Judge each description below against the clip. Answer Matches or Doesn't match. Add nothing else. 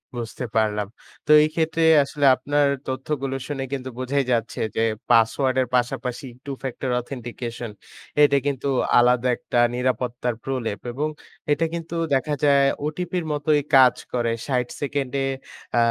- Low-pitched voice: Matches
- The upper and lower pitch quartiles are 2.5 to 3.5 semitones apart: Matches